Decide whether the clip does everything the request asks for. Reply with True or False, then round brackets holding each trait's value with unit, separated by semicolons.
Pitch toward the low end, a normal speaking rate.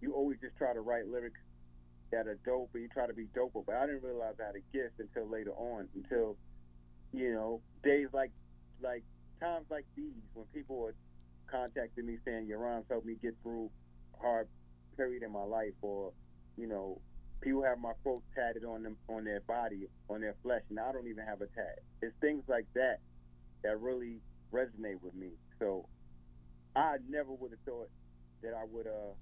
True (110 Hz; 195 wpm)